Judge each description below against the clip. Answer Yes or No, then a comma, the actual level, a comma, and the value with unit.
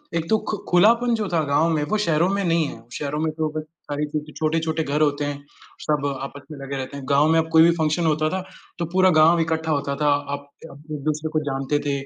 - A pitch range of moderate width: No, narrow, 2.2 semitones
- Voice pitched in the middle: Yes, medium, 155 Hz